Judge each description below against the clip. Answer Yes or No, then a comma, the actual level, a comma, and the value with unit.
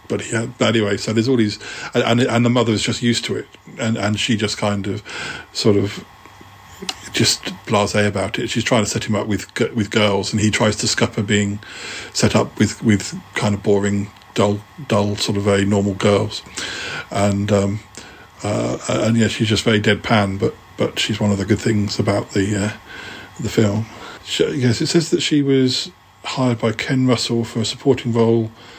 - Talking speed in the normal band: Yes, average, 195 wpm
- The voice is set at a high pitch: No, low, 110 Hz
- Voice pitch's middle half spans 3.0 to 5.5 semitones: No, narrow, 2.4 semitones